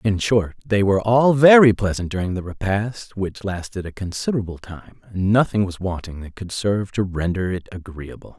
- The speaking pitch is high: No, low, 100 Hz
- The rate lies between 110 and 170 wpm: No, average, 185 wpm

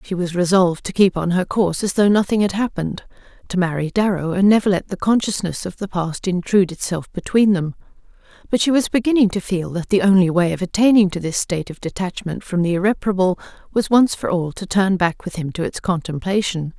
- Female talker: Yes, female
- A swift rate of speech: Yes, fast, 215 wpm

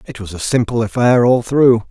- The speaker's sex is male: Yes, male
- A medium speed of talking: No, fast, 220 wpm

